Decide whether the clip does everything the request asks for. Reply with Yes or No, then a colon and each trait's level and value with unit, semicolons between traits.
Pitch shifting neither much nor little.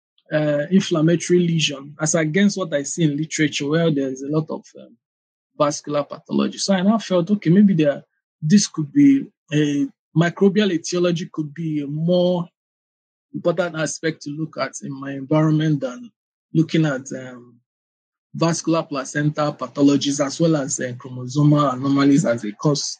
Yes: average, 3.3 semitones